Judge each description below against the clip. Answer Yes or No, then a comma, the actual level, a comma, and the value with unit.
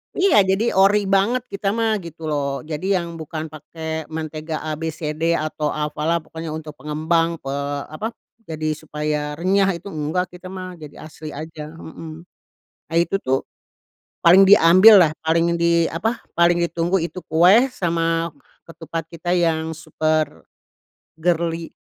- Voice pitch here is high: No, medium, 165 Hz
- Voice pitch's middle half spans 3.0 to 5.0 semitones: No, narrow, 2.5 semitones